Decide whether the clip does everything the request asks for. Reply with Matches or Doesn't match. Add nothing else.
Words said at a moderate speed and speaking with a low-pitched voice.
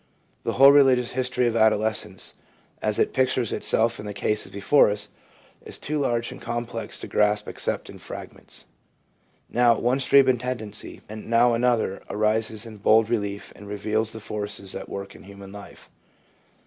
Matches